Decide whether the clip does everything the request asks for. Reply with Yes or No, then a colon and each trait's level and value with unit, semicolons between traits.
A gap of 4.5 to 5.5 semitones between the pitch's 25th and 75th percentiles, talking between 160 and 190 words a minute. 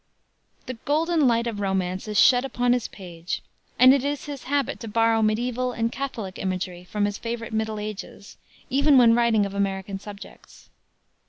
No: average, 3.9 semitones; average, 170 wpm